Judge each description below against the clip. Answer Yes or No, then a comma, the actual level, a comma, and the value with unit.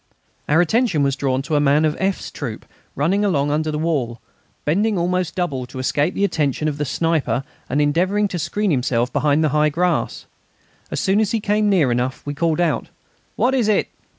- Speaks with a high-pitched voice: No, medium, 155 Hz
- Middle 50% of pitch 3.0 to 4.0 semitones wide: No, average, 4.9 semitones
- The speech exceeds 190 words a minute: Yes, average, 200 wpm